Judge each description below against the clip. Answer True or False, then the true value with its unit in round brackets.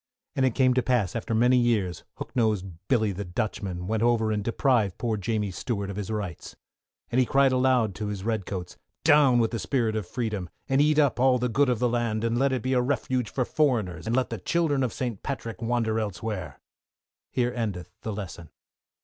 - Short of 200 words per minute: False (205 wpm)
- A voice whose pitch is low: True (115 Hz)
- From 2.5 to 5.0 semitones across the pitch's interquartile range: True (3.5 semitones)